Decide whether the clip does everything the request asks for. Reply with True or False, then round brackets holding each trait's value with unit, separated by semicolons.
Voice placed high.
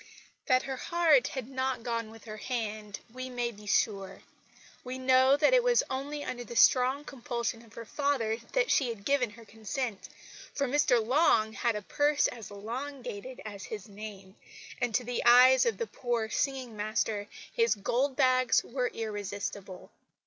True (245 Hz)